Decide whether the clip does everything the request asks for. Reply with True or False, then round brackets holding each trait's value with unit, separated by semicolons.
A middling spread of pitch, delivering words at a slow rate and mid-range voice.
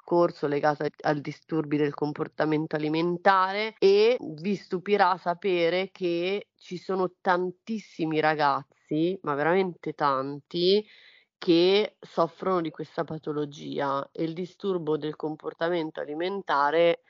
True (3.4 semitones; 100 wpm; 170 Hz)